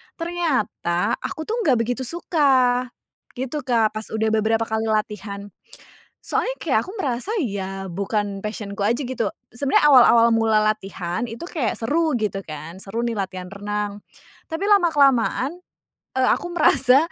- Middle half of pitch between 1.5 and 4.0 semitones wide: No, average, 5.0 semitones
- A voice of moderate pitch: No, high, 225 Hz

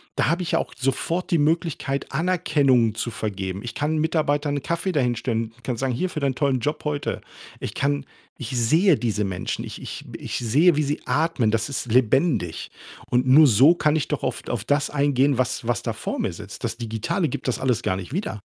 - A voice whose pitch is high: No, low, 135 Hz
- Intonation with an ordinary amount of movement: Yes, average, 4.5 semitones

